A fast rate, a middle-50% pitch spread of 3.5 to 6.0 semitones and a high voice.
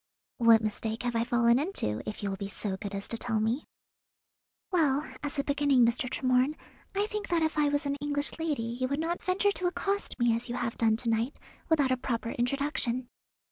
Yes: fast, 215 wpm; average, 4.3 semitones; very high, 255 Hz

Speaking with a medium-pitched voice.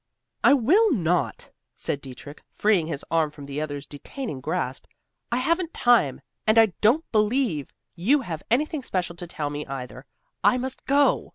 Yes: medium, 180 Hz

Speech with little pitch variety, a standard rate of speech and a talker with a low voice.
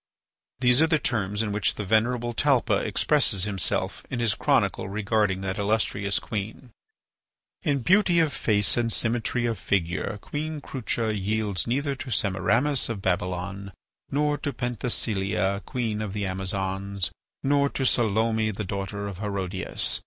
No: average, 3.9 semitones; average, 145 wpm; low, 110 Hz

